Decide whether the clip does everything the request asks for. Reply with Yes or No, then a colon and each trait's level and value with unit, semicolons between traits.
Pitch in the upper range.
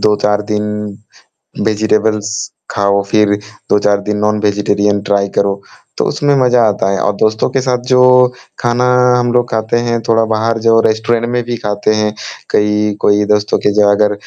No: low, 105 Hz